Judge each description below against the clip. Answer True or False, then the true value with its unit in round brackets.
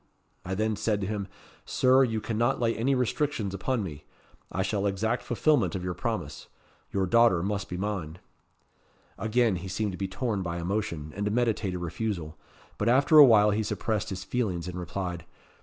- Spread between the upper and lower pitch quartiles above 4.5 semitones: False (3.9 semitones)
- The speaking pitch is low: True (105 Hz)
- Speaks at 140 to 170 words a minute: False (185 wpm)